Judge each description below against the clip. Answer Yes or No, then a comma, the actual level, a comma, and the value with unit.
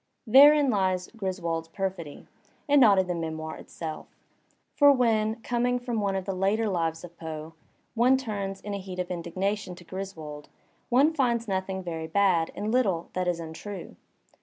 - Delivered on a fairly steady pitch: No, average, 4.7 semitones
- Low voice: No, high, 190 Hz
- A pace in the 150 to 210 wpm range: Yes, average, 165 wpm